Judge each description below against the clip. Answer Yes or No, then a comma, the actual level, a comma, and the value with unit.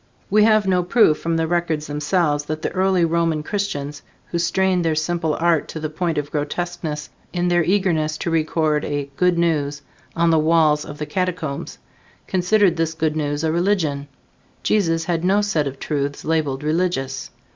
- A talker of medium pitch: Yes, medium, 165 Hz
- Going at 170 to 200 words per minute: Yes, average, 175 wpm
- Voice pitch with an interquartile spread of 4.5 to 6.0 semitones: No, average, 2.8 semitones